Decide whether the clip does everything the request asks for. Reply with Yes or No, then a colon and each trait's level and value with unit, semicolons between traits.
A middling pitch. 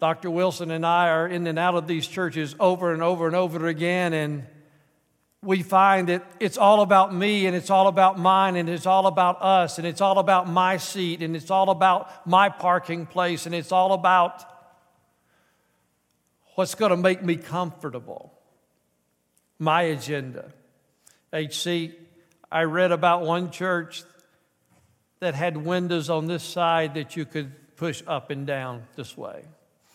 Yes: medium, 175 Hz